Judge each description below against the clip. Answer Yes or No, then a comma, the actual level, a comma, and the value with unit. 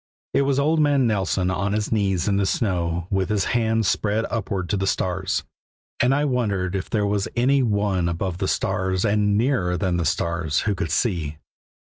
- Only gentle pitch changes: No, average, 3.6 semitones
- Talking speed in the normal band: Yes, average, 195 wpm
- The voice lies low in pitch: Yes, low, 100 Hz